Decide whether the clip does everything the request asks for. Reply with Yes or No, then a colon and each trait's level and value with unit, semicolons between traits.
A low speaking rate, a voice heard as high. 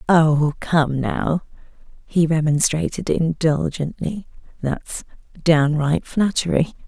No: slow, 70 wpm; medium, 155 Hz